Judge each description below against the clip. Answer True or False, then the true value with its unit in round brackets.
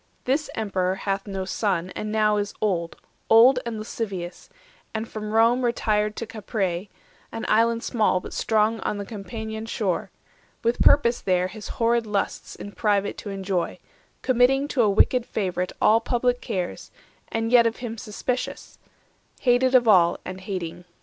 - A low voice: False (215 Hz)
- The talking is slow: False (160 wpm)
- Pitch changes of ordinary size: True (3.1 semitones)